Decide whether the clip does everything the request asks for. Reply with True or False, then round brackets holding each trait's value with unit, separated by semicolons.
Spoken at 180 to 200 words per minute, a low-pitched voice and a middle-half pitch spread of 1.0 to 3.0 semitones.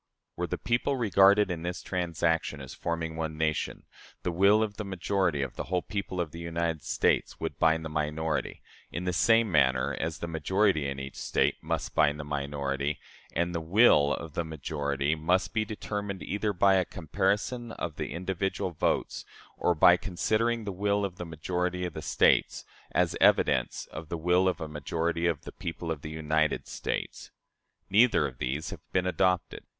False (185 wpm; 85 Hz; 3.7 semitones)